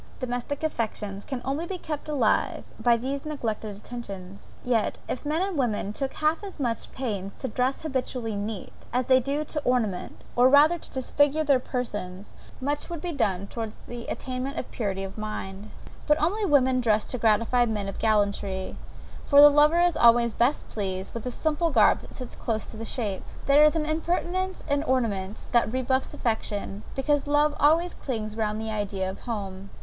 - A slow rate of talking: No, average, 185 wpm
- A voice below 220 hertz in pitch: No, high, 245 Hz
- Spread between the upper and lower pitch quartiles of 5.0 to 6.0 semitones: Yes, wide, 5.4 semitones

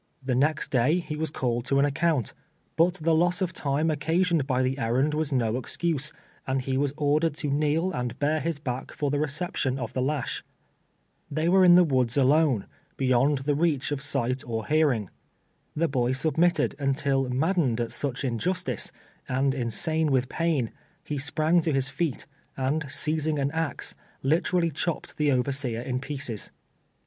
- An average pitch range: Yes, average, 3.4 semitones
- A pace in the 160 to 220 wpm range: Yes, average, 175 wpm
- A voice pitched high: No, medium, 145 Hz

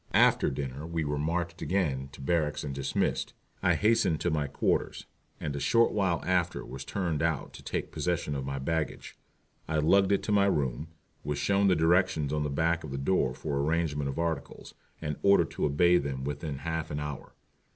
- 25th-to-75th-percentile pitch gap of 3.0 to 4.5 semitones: Yes, average, 3.6 semitones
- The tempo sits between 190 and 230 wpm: Yes, average, 195 wpm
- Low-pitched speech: Yes, very low, 80 Hz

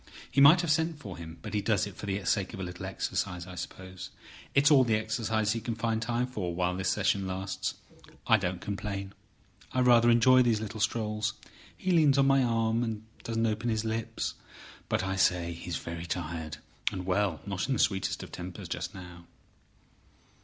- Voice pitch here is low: Yes, low, 105 Hz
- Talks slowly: No, average, 190 wpm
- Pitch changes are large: No, average, 4.1 semitones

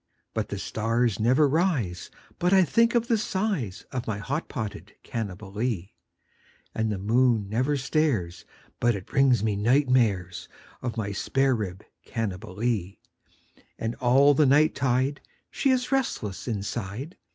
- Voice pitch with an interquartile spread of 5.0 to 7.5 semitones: Yes, wide, 5.5 semitones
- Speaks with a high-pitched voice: No, low, 120 Hz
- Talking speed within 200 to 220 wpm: No, average, 140 wpm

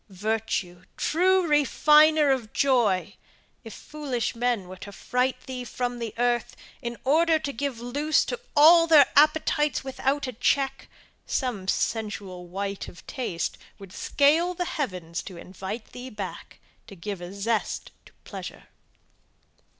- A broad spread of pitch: Yes, wide, 6.5 semitones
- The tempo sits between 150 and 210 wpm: No, slow, 135 wpm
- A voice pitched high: Yes, high, 245 Hz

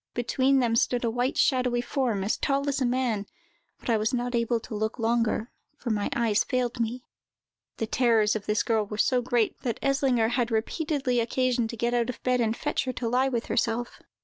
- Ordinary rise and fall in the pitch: No, narrow, 2.0 semitones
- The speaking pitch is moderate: No, high, 240 Hz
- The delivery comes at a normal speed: No, fast, 210 wpm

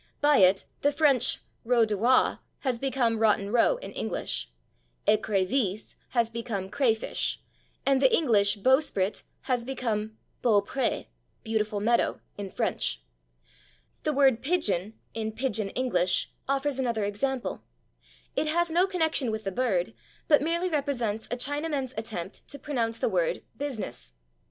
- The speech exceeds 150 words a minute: No, slow, 135 wpm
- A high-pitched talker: Yes, high, 235 Hz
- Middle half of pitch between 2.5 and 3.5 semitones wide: No, average, 4.6 semitones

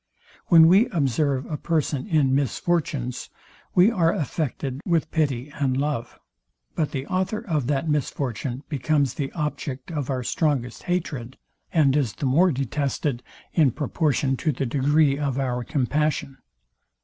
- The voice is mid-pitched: Yes, medium, 145 Hz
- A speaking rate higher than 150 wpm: No, average, 140 wpm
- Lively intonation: No, average, 3.1 semitones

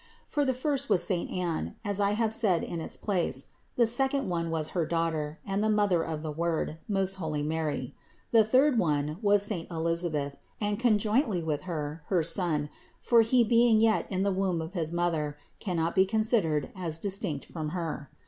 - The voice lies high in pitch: No, medium, 180 Hz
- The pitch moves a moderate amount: Yes, average, 4.8 semitones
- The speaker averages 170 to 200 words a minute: Yes, average, 195 wpm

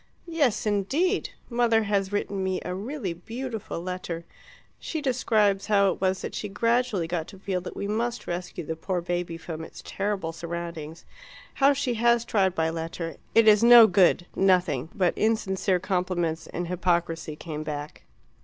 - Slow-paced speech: No, average, 165 wpm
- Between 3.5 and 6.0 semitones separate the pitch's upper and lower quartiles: Yes, average, 4.5 semitones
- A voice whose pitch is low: No, high, 190 Hz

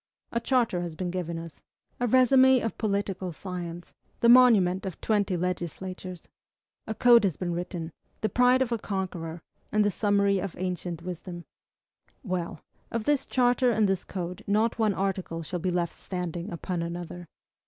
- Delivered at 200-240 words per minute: No, average, 165 wpm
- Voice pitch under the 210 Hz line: Yes, medium, 185 Hz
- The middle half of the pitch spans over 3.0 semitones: Yes, average, 3.9 semitones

